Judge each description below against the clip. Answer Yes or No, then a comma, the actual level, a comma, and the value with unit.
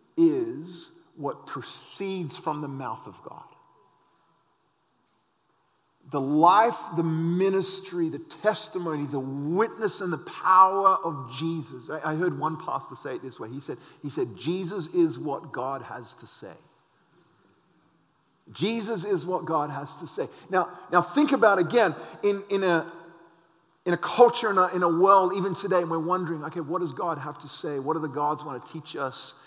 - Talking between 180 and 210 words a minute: No, average, 170 wpm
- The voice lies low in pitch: No, medium, 170 Hz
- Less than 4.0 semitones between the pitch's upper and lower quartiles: Yes, average, 3.6 semitones